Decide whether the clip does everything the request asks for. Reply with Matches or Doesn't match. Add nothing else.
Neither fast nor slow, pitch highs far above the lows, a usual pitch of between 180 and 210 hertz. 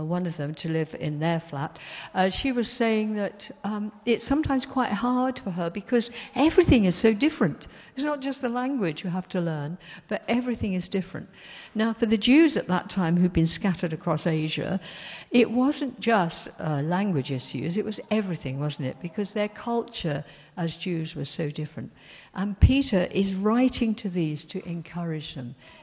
Matches